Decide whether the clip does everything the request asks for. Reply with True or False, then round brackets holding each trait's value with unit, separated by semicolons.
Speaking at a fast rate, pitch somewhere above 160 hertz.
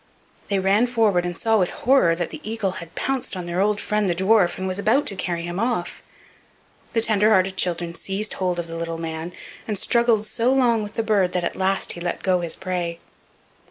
True (220 wpm; 190 Hz)